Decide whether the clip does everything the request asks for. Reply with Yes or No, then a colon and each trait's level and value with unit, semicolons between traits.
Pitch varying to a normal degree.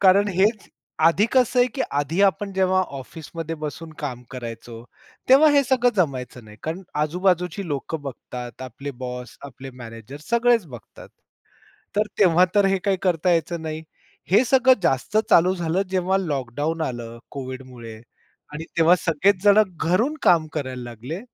No: wide, 6.8 semitones